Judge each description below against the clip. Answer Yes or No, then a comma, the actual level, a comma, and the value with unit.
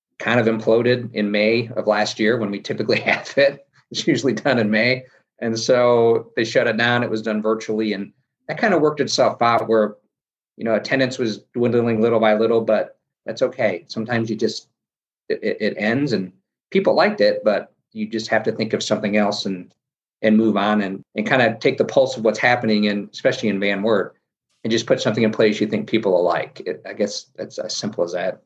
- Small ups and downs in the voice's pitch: Yes, narrow, 2.3 semitones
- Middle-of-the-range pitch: No, low, 110 Hz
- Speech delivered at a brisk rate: Yes, fast, 220 wpm